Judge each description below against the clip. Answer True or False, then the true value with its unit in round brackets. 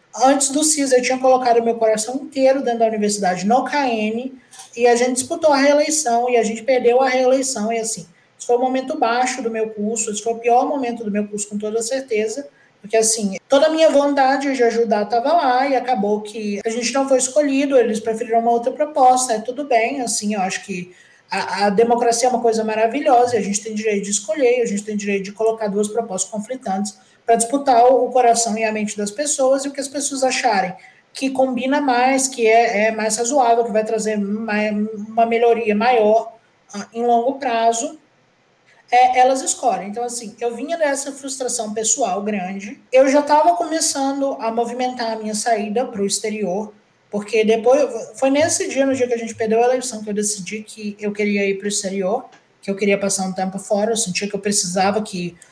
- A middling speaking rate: False (210 wpm)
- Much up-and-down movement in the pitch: False (3.3 semitones)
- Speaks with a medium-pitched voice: False (235 Hz)